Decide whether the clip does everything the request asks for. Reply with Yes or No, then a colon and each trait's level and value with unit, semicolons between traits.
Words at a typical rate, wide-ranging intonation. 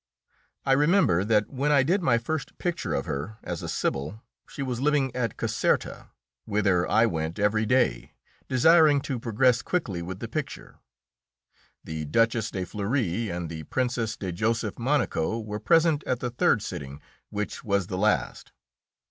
Yes: average, 160 wpm; wide, 5.7 semitones